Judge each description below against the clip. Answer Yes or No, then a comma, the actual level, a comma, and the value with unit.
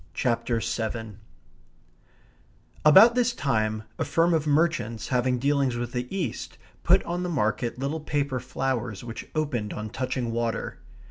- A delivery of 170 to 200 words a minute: No, average, 140 wpm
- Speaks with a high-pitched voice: No, low, 125 Hz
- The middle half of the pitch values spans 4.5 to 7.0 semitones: Yes, average, 4.9 semitones